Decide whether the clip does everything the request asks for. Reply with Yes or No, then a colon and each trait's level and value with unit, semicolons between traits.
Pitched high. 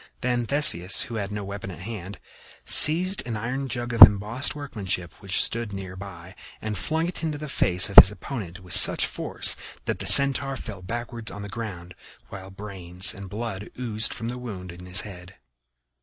No: low, 105 Hz